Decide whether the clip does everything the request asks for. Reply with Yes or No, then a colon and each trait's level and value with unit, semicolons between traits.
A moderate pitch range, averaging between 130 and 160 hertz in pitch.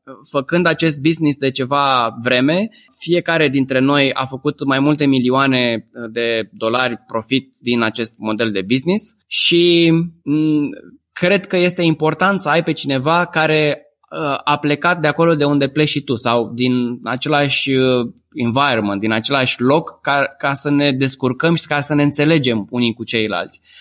Yes: average, 3.9 semitones; medium, 140 Hz